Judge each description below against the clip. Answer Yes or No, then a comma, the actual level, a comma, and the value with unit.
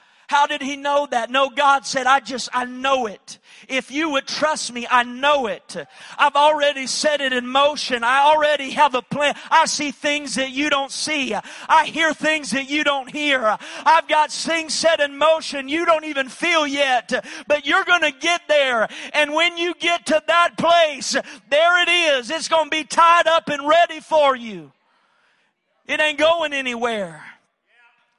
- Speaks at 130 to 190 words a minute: Yes, average, 185 wpm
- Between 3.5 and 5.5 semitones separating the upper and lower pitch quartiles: No, average, 3.0 semitones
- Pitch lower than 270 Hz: No, very high, 290 Hz